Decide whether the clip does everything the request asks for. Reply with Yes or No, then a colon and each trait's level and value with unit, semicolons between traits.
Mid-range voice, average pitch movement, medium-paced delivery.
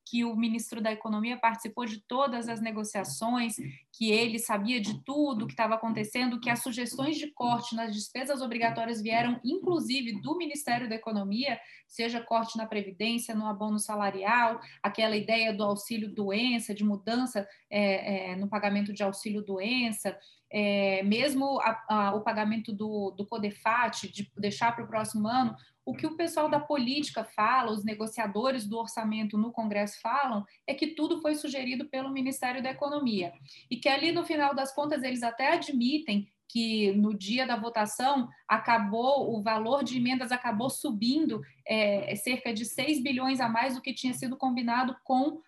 No: high, 230 Hz; average, 3.3 semitones; average, 165 wpm